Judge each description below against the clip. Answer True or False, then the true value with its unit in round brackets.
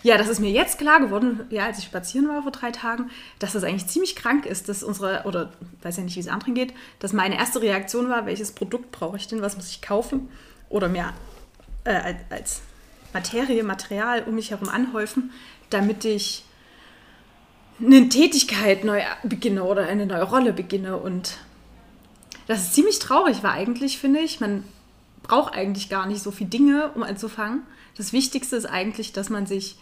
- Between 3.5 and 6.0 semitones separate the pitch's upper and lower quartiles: True (4.1 semitones)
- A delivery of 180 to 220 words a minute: True (185 wpm)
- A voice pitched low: False (215 Hz)